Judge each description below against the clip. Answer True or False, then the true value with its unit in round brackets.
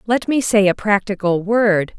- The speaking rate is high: False (180 wpm)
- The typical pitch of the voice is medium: False (205 Hz)